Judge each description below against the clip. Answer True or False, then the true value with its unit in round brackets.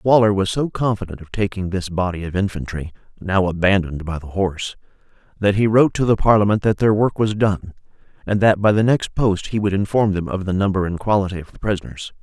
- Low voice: True (100 Hz)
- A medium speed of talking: False (215 wpm)